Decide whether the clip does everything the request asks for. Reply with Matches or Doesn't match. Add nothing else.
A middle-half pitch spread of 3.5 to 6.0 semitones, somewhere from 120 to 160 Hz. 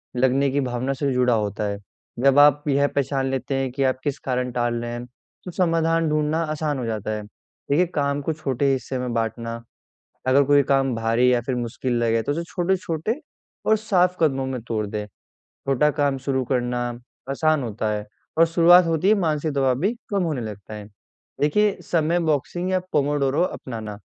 Matches